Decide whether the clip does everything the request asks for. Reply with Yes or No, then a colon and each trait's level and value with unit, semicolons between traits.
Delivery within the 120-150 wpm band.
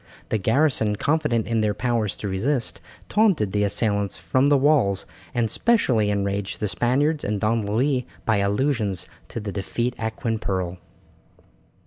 Yes: average, 145 wpm